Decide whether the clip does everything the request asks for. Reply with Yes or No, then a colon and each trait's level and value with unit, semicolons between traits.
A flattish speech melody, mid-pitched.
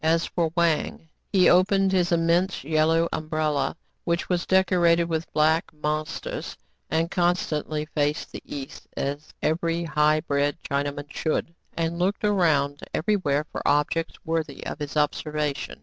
Yes: narrow, 2.3 semitones; medium, 160 Hz